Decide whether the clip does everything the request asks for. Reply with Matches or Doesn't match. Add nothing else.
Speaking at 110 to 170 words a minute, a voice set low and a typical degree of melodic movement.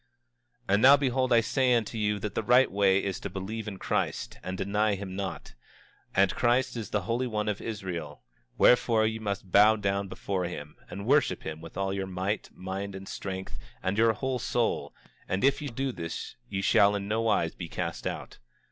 Doesn't match